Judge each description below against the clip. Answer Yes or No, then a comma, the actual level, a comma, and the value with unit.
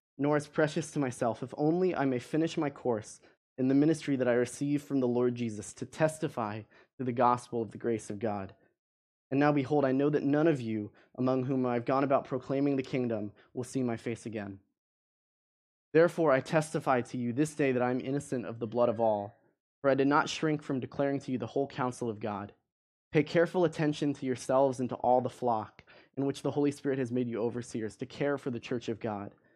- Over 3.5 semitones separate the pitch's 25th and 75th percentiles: No, average, 3.2 semitones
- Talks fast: Yes, fast, 225 wpm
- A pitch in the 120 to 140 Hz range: Yes, low, 130 Hz